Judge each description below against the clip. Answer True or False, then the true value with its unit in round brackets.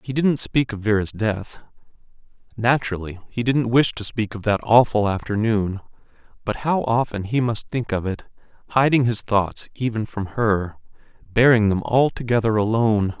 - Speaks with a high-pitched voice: False (110 Hz)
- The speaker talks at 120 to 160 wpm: True (155 wpm)